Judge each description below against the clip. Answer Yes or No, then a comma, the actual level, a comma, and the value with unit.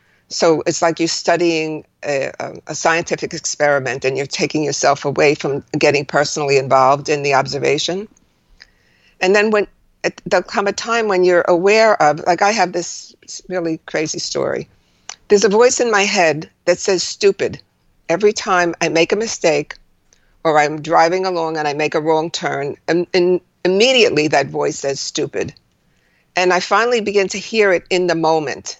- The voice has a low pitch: No, medium, 175 Hz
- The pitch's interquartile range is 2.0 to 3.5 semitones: No, average, 4.7 semitones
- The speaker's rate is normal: Yes, average, 170 wpm